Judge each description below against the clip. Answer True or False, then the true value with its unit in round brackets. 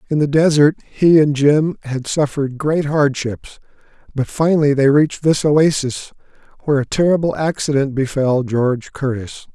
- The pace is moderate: True (145 wpm)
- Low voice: False (145 Hz)